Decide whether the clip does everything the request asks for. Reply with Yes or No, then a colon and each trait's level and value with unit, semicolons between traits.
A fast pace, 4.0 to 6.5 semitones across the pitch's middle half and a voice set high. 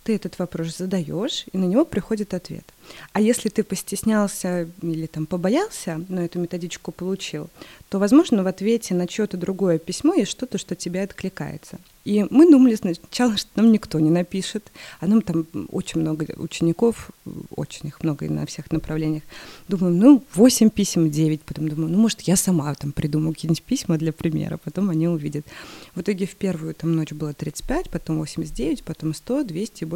No: fast, 180 wpm; average, 4.4 semitones; medium, 180 Hz